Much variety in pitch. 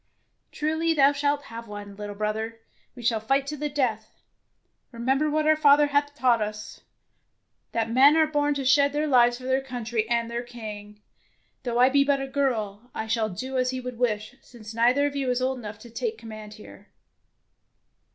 No: average, 4.3 semitones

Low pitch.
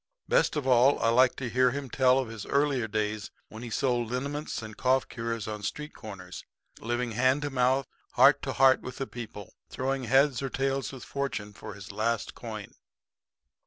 Yes: low, 125 Hz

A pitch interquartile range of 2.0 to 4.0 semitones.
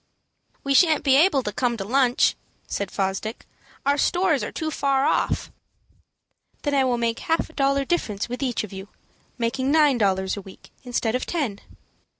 No: average, 4.6 semitones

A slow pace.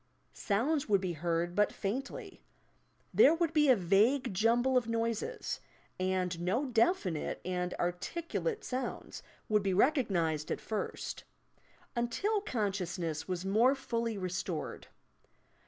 Yes: slow, 120 wpm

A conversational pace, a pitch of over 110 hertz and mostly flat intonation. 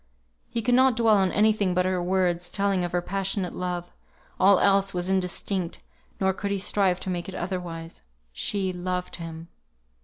Yes: average, 180 wpm; medium, 185 Hz; narrow, 1.8 semitones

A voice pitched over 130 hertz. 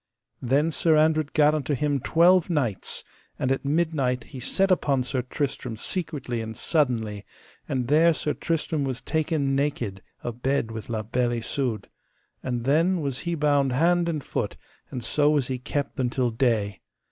Yes: medium, 140 Hz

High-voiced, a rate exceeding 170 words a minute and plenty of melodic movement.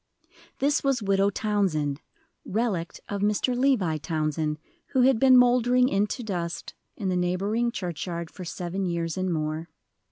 No: high, 195 Hz; average, 140 wpm; wide, 5.9 semitones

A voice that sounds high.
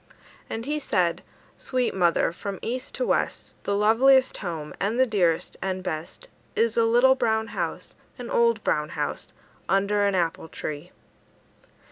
Yes: high, 210 Hz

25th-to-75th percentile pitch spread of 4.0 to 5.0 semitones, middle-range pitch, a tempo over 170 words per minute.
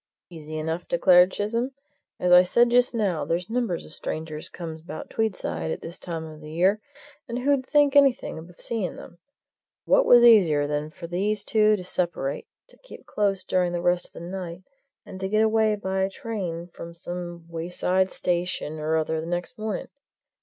Yes: average, 4.3 semitones; medium, 180 Hz; average, 180 wpm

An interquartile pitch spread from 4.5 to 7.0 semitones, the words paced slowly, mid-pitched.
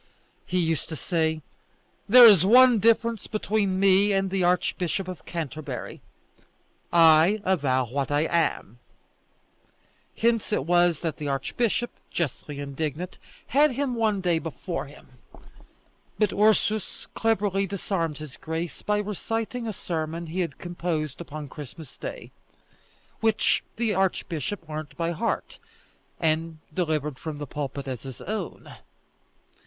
Yes: average, 5.1 semitones; slow, 130 wpm; medium, 175 Hz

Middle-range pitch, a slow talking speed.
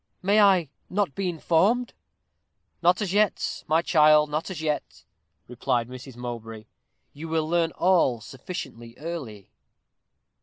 Yes: medium, 160 Hz; slow, 125 wpm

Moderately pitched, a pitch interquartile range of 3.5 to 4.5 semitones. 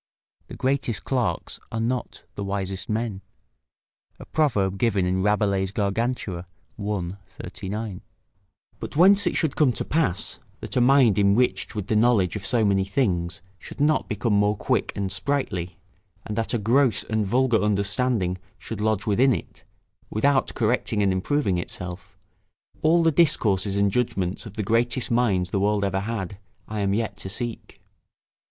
No: low, 105 Hz; average, 3.9 semitones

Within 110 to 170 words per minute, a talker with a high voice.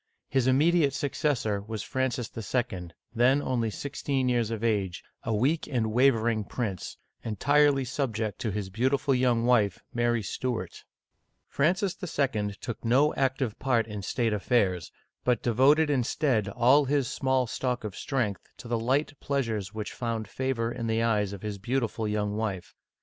No: average, 160 wpm; low, 120 Hz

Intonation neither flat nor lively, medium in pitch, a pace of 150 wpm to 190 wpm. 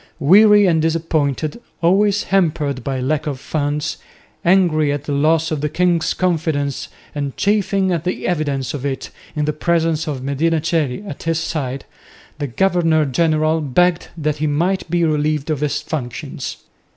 Yes: average, 3.0 semitones; medium, 155 Hz; average, 160 wpm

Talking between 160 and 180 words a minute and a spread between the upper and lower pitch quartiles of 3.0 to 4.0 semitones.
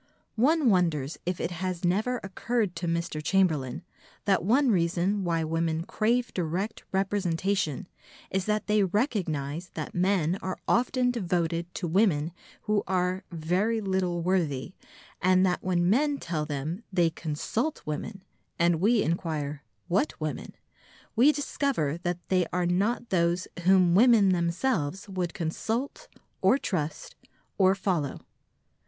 No: slow, 135 wpm; average, 3.7 semitones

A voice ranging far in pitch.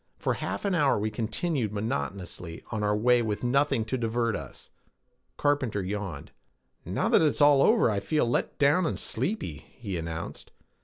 Yes: wide, 5.8 semitones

